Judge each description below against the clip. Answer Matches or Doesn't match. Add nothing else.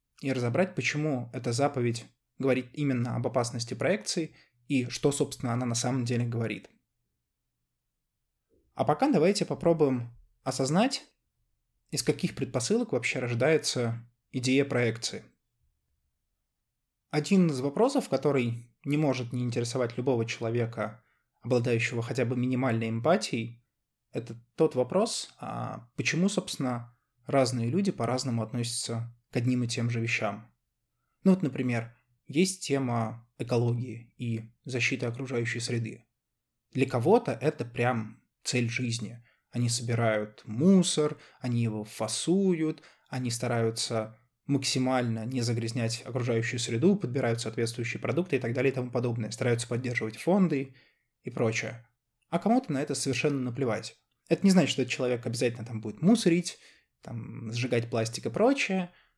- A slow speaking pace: Doesn't match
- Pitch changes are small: Doesn't match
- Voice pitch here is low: Matches